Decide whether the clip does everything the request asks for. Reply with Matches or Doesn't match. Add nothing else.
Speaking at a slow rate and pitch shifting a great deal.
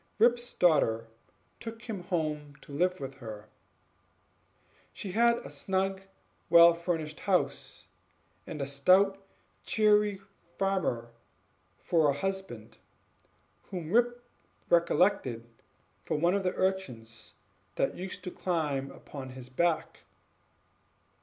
Matches